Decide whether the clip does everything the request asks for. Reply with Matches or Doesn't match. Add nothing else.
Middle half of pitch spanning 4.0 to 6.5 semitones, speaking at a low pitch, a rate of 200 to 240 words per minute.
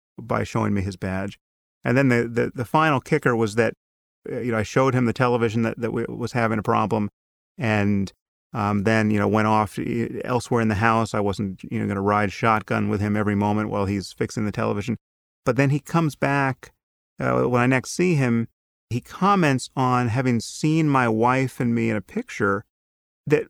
Doesn't match